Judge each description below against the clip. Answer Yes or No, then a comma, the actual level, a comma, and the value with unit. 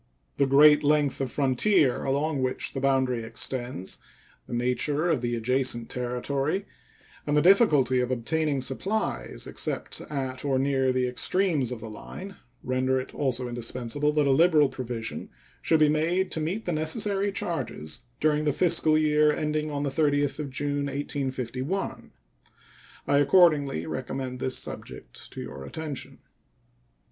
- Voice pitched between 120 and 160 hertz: Yes, medium, 140 Hz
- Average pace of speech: Yes, average, 145 wpm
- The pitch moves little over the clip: No, average, 3.2 semitones